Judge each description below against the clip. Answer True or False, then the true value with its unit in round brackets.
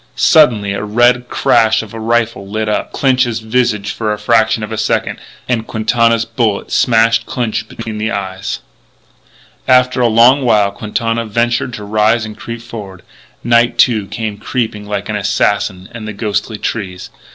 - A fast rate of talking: False (165 wpm)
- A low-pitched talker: True (110 Hz)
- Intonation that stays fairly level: True (1.9 semitones)